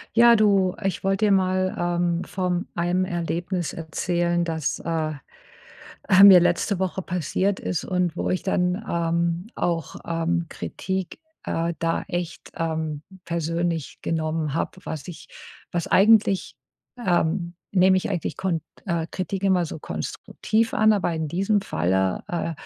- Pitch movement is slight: Yes, narrow, 2.3 semitones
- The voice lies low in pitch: No, medium, 175 Hz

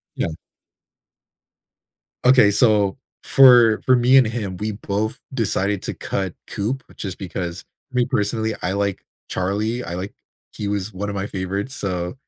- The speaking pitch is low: Yes, low, 105 Hz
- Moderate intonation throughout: Yes, average, 3.2 semitones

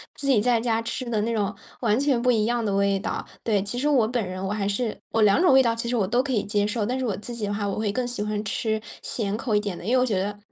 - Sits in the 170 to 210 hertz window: No, high, 220 Hz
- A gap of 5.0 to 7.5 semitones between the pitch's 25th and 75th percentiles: No, average, 2.9 semitones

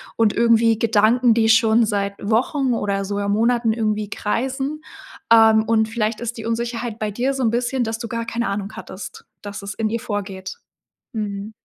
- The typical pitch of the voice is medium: No, high, 225 Hz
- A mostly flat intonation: Yes, narrow, 2.1 semitones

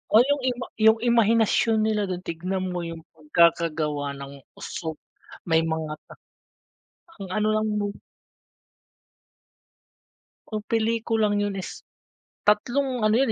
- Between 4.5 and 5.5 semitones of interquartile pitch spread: Yes, average, 5.1 semitones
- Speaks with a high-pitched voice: Yes, high, 205 Hz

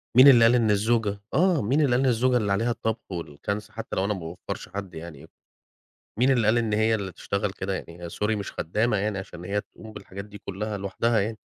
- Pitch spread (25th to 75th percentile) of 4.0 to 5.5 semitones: No, average, 2.9 semitones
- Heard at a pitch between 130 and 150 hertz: No, low, 105 Hz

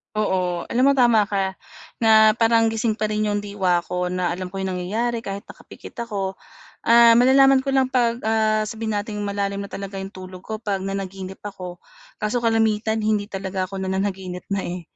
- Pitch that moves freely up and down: No, average, 2.7 semitones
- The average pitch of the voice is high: Yes, high, 205 Hz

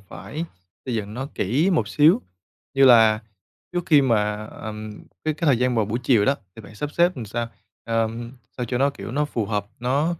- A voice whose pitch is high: No, low, 120 Hz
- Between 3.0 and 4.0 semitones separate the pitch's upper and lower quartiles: No, average, 4.7 semitones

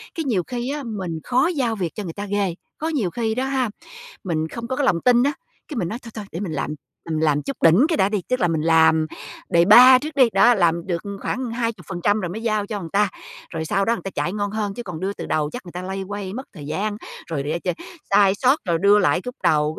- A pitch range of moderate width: No, wide, 5.9 semitones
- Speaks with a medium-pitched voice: No, high, 200 Hz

